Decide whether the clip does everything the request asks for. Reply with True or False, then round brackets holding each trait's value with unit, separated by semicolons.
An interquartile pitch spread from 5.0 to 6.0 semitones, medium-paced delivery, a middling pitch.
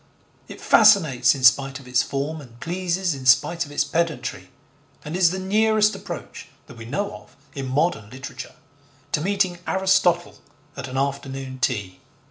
True (5.5 semitones; 160 wpm; 145 Hz)